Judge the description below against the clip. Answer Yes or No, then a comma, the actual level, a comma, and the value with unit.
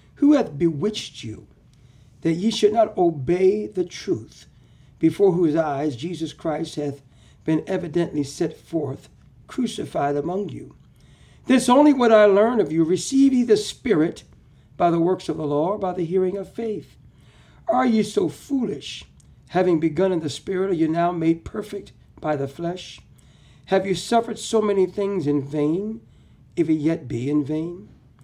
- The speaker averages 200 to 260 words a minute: No, average, 165 wpm